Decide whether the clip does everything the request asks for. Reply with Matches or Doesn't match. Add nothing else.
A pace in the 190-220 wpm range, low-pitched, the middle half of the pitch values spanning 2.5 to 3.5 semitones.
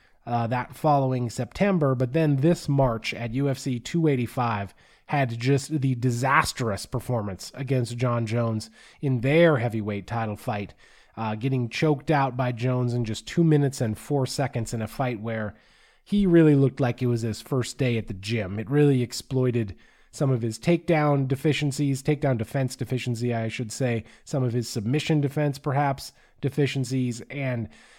Doesn't match